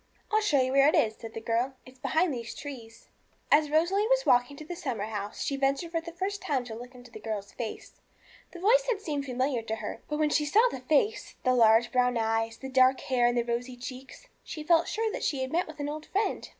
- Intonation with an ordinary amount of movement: Yes, average, 4.9 semitones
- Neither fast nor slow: No, fast, 245 wpm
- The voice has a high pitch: Yes, very high, 265 Hz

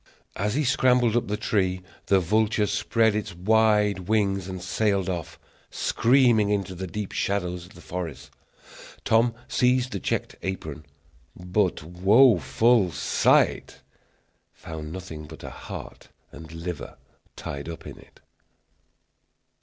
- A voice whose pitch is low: Yes, low, 100 Hz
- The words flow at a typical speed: No, slow, 130 wpm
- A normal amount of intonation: Yes, average, 3.9 semitones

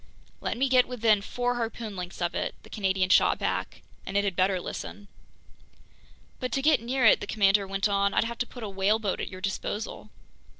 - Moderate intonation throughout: Yes, average, 3.5 semitones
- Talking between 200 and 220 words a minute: Yes, fast, 205 wpm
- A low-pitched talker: No, high, 205 Hz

